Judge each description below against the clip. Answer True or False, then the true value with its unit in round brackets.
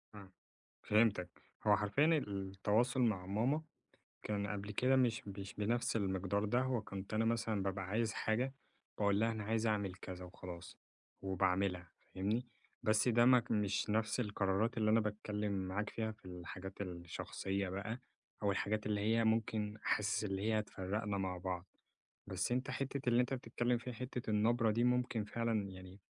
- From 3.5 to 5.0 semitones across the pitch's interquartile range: False (2.9 semitones)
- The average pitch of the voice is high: False (105 Hz)